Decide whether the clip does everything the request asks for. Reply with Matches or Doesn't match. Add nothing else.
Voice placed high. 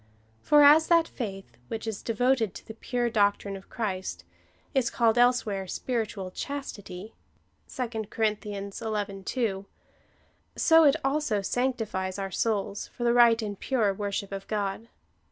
Matches